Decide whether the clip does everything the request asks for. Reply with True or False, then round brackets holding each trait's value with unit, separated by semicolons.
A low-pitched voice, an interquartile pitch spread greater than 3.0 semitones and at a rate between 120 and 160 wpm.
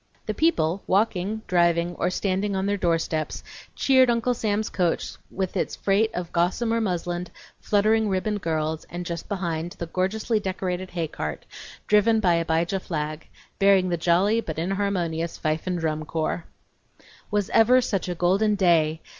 False (185 Hz; 3.6 semitones; 150 wpm)